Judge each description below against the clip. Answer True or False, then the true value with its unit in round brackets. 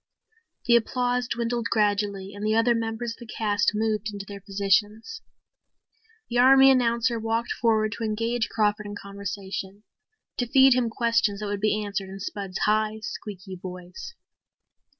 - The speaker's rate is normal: True (150 wpm)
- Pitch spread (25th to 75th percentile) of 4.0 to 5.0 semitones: False (2.6 semitones)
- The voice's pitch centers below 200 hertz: False (215 Hz)